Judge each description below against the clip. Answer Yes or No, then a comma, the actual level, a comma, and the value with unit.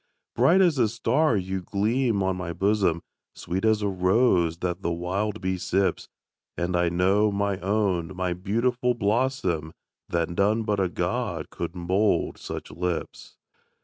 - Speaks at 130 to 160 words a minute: Yes, average, 150 wpm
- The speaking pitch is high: No, very low, 95 Hz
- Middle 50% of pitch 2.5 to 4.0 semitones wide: Yes, average, 3.3 semitones